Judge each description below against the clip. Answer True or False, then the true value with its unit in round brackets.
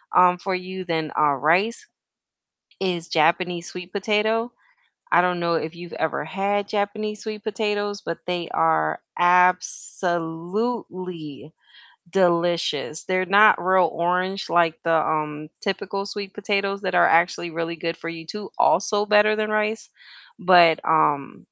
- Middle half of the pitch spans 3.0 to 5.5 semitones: True (3.4 semitones)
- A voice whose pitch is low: False (180 Hz)